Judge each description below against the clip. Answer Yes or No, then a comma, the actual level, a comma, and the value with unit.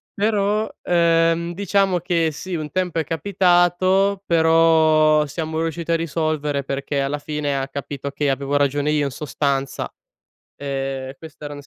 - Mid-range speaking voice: Yes, medium, 155 Hz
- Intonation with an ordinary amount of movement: Yes, average, 3.3 semitones